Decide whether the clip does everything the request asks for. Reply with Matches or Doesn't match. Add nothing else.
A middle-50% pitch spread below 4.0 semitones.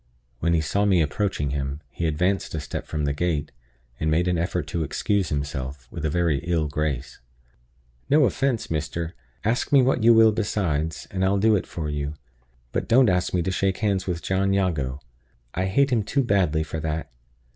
Doesn't match